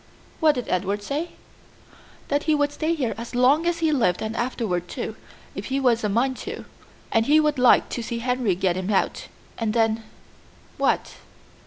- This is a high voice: Yes, high, 245 Hz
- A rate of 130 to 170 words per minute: No, average, 190 wpm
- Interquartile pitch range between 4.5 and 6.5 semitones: Yes, average, 4.9 semitones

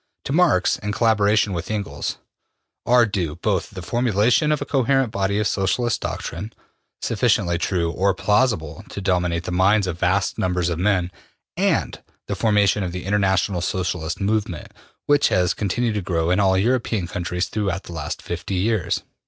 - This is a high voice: No, very low, 95 Hz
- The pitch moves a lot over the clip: No, average, 3.3 semitones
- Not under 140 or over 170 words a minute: Yes, average, 165 wpm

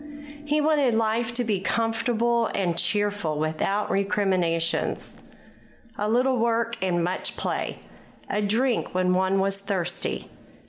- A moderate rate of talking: No, slow, 125 wpm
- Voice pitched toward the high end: Yes, high, 205 Hz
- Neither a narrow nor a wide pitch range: Yes, average, 4.0 semitones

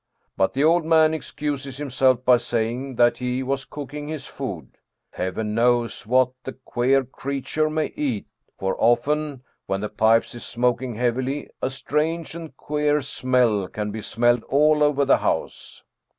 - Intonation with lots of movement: No, average, 3.7 semitones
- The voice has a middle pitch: No, low, 130 Hz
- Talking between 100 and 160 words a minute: Yes, average, 155 wpm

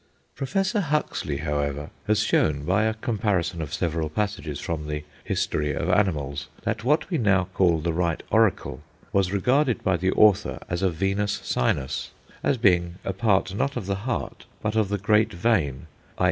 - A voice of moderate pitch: No, very low, 95 Hz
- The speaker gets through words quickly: No, average, 175 wpm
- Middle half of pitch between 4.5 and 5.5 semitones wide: Yes, average, 5.2 semitones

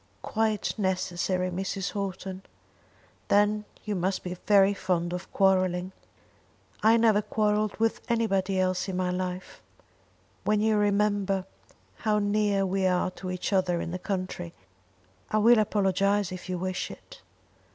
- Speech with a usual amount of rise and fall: No, narrow, 2.2 semitones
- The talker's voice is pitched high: Yes, high, 195 Hz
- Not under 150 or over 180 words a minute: No, average, 140 wpm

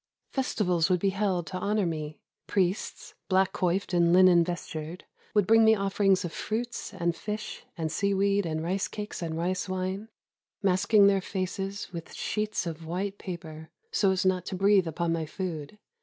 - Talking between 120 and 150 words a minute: No, average, 170 wpm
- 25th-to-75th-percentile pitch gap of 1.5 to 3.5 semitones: Yes, average, 2.7 semitones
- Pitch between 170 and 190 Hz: Yes, medium, 185 Hz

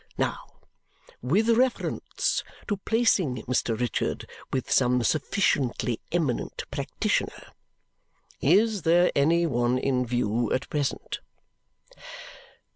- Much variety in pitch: Yes, wide, 7.1 semitones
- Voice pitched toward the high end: No, medium, 140 Hz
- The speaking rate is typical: No, slow, 95 wpm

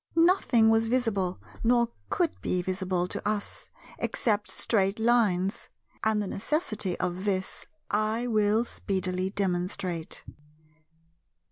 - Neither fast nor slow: No, slow, 110 wpm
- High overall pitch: Yes, high, 205 Hz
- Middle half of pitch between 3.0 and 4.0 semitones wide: Yes, average, 3.4 semitones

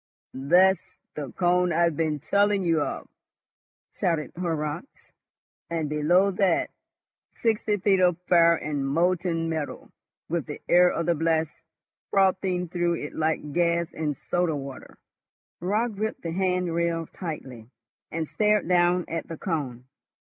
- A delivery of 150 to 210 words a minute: No, slow, 135 wpm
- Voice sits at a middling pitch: Yes, medium, 170 Hz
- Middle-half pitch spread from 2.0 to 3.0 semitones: Yes, narrow, 2.6 semitones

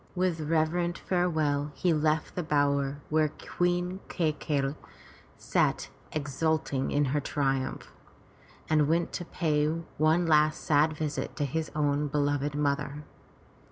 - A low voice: No, medium, 150 Hz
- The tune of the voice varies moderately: No, narrow, 2.0 semitones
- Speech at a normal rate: No, slow, 125 wpm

